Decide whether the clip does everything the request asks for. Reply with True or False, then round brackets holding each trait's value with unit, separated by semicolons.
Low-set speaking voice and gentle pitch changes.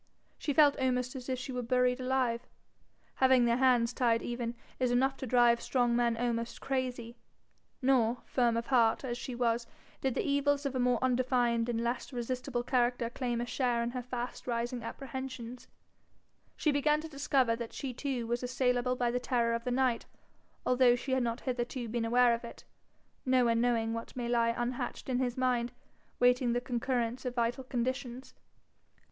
False (245 Hz; 1.4 semitones)